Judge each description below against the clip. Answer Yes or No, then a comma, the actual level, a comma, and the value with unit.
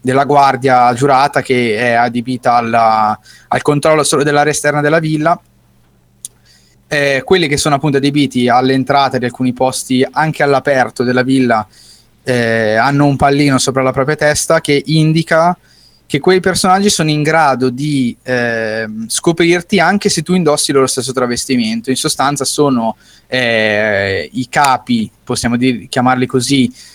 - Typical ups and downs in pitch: Yes, average, 3.2 semitones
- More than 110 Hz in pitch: Yes, low, 135 Hz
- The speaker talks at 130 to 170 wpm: Yes, average, 140 wpm